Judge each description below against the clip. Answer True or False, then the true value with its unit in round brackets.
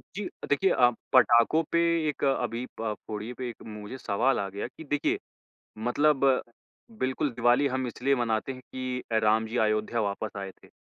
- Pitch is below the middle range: True (120 Hz)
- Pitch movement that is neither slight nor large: True (3.5 semitones)